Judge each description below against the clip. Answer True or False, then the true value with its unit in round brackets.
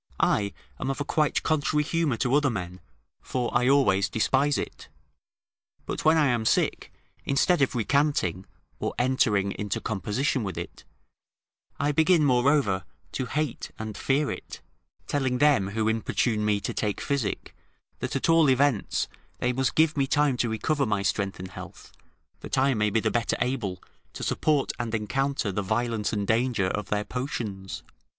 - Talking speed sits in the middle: True (165 wpm)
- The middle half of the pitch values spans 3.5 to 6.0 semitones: True (5.1 semitones)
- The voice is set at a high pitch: False (125 Hz)